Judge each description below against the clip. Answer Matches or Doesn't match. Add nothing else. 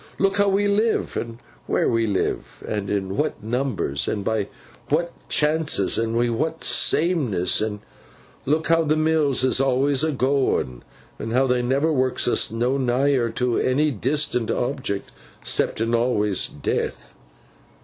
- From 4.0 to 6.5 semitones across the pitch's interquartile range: Matches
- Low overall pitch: Matches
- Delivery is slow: Doesn't match